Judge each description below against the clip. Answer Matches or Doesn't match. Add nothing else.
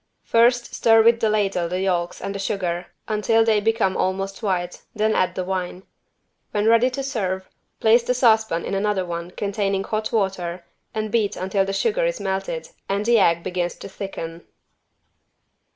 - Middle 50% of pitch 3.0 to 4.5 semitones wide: Matches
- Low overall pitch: Doesn't match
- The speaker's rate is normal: Matches